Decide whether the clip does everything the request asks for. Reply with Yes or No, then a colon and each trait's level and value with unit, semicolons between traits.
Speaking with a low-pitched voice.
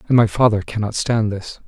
Yes: low, 110 Hz